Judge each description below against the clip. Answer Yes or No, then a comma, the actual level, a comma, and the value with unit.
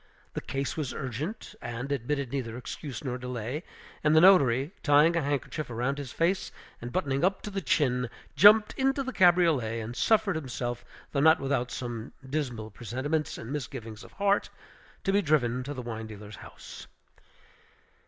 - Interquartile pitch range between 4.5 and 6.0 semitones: Yes, average, 4.8 semitones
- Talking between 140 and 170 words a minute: Yes, average, 165 wpm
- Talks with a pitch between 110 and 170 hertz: Yes, medium, 140 Hz